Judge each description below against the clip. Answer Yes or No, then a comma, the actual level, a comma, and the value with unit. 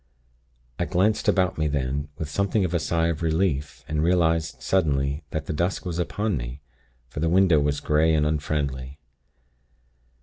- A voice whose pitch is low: Yes, very low, 80 Hz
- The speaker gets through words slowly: No, average, 165 wpm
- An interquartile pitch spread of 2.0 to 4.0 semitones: Yes, average, 3.2 semitones